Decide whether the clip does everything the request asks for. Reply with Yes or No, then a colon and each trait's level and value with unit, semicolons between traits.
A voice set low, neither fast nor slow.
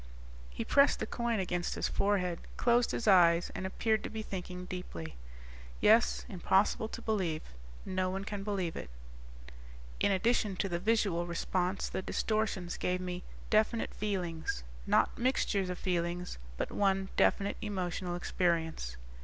No: medium, 185 Hz; average, 145 wpm